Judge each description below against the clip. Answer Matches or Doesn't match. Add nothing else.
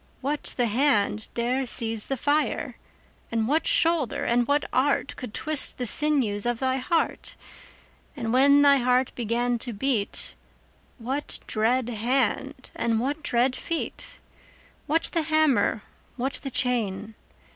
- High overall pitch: Matches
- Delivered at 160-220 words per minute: Doesn't match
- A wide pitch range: Doesn't match